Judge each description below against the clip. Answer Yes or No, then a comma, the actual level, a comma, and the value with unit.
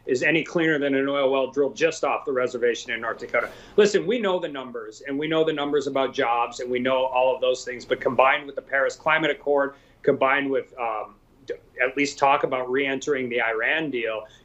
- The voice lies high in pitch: No, medium, 140 Hz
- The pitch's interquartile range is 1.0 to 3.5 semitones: No, average, 4.3 semitones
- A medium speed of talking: No, fast, 220 wpm